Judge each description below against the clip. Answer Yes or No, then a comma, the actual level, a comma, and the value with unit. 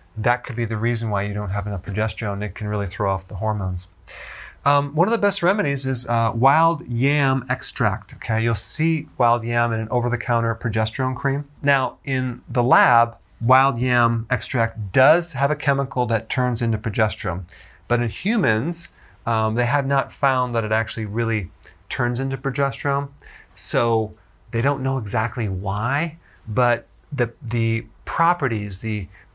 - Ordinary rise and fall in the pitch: Yes, average, 3.8 semitones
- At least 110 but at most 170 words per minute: Yes, average, 165 wpm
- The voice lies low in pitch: Yes, low, 120 Hz